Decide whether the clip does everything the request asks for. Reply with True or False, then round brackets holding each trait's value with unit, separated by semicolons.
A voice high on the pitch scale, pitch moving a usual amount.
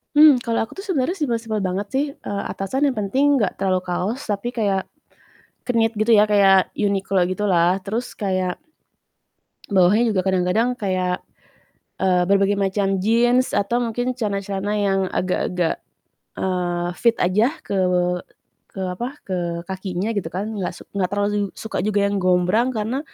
True (200 Hz; 3.6 semitones)